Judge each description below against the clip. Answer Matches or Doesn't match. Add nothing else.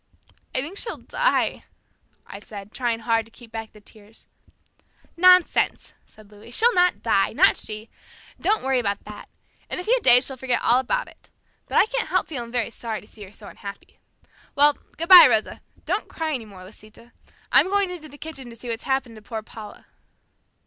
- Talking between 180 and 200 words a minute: Matches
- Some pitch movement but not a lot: Doesn't match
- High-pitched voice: Matches